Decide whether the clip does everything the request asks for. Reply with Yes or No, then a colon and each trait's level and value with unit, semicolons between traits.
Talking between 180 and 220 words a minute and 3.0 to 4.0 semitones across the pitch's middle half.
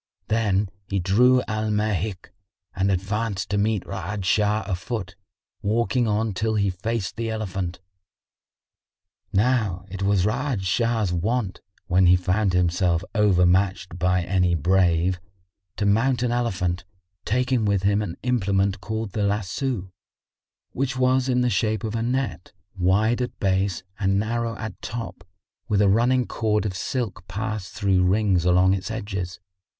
No: average, 145 wpm; average, 3.3 semitones